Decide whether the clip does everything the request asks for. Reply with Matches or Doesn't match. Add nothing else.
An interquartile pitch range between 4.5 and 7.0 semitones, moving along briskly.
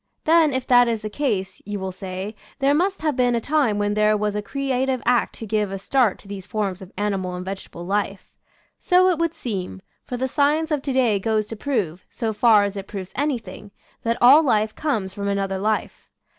Matches